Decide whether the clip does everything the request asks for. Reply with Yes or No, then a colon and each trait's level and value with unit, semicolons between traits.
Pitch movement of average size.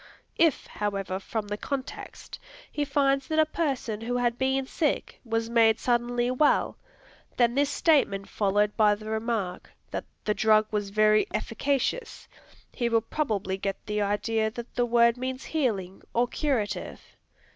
Yes: average, 3.9 semitones